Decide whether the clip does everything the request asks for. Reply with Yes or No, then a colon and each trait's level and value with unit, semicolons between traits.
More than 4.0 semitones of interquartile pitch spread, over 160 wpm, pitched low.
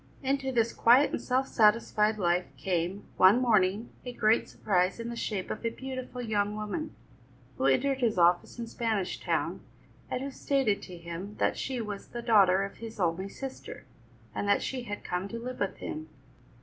No: average, 4.5 semitones; average, 185 wpm; high, 215 Hz